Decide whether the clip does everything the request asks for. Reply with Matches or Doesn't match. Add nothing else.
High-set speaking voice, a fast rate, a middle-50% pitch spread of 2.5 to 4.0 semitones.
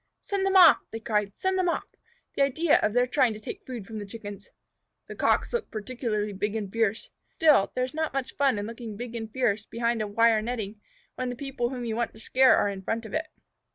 Matches